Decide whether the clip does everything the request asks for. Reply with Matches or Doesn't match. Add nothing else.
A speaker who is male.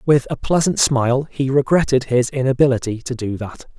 Matches